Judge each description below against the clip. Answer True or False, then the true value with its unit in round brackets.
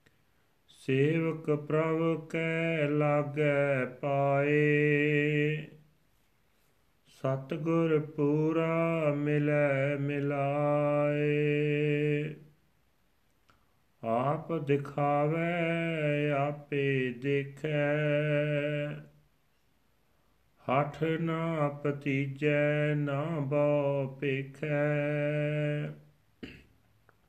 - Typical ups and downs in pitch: False (1.0 semitones)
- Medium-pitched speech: True (145 Hz)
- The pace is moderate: False (40 wpm)